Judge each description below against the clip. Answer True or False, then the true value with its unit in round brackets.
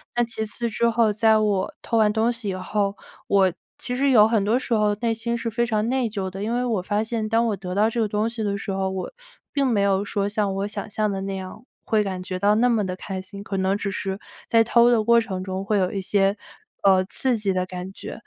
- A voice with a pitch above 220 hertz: False (210 Hz)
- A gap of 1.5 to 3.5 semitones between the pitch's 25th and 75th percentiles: True (2.8 semitones)